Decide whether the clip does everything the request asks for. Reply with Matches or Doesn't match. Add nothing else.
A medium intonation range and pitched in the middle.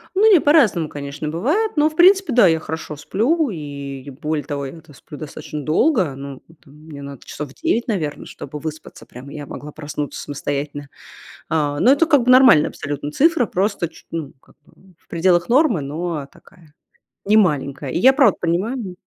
Doesn't match